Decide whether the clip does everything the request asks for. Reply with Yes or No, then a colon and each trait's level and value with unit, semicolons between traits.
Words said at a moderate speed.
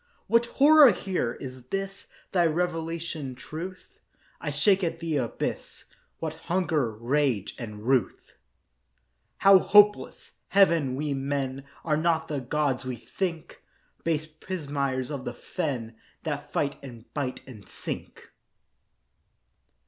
No: slow, 120 wpm